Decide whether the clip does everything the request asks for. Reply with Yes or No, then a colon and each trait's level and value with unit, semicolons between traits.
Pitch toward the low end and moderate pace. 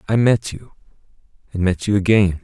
Yes: low, 100 Hz; average, 175 wpm